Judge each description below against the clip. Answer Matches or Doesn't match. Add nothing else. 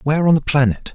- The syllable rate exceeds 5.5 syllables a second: Matches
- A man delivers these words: Matches